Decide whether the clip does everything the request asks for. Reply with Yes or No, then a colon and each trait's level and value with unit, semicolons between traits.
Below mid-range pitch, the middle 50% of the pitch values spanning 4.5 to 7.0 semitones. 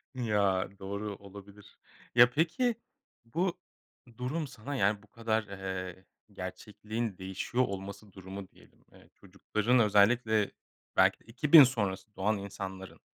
No: low, 105 Hz; average, 3.7 semitones